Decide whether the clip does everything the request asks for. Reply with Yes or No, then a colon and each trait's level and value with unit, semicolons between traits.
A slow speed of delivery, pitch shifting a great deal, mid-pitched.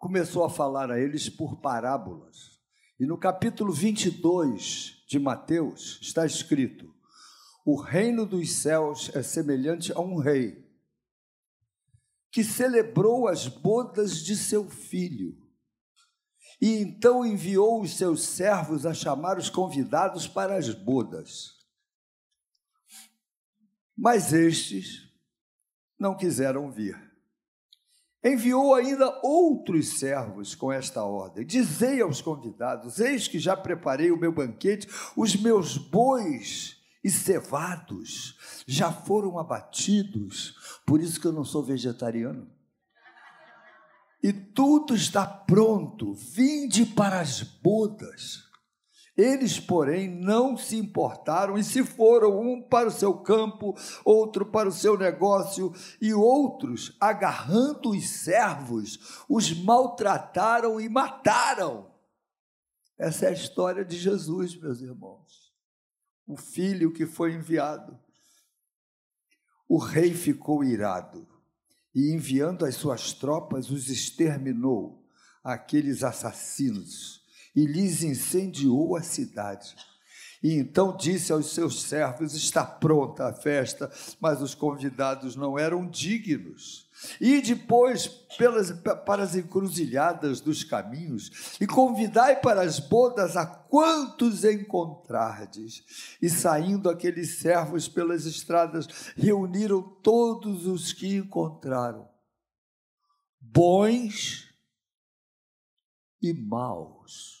Yes: slow, 110 wpm; wide, 6.4 semitones; medium, 180 Hz